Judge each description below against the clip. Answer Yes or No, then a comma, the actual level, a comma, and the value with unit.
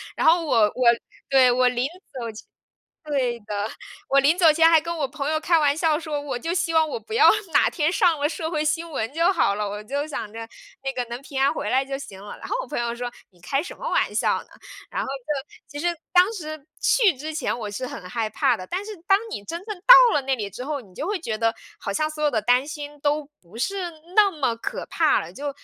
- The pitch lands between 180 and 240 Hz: No, very high, 290 Hz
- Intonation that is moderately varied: Yes, average, 4.9 semitones